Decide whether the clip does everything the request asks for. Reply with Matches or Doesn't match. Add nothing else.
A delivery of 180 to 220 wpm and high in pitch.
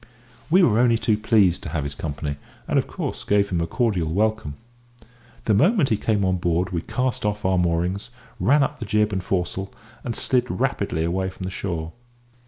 Doesn't match